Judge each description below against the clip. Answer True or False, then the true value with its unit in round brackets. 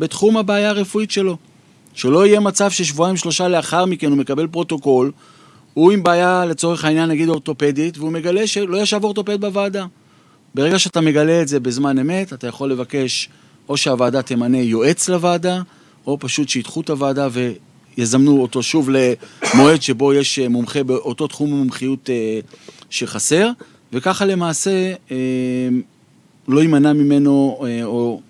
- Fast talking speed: False (135 wpm)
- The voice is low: False (150 Hz)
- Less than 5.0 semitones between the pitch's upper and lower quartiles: False (5.4 semitones)